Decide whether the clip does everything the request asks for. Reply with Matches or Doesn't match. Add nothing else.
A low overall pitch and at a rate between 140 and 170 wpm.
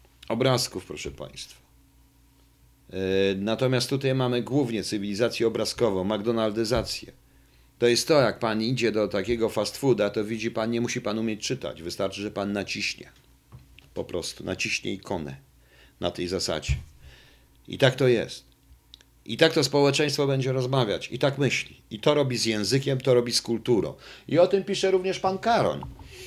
Matches